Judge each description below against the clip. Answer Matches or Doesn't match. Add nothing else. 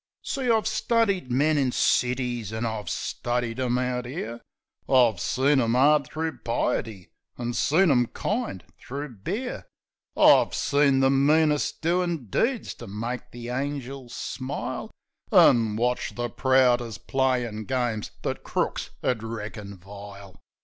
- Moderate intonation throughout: Matches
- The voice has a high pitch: Doesn't match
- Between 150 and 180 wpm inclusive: Doesn't match